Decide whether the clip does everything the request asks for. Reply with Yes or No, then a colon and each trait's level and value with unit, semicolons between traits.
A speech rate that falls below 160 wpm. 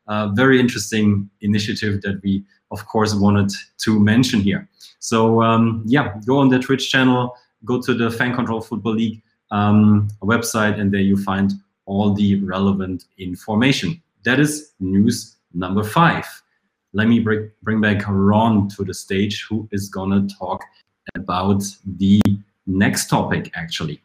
Yes: average, 150 wpm